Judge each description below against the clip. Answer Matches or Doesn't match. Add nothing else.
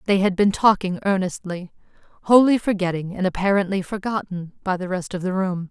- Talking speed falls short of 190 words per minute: Matches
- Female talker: Matches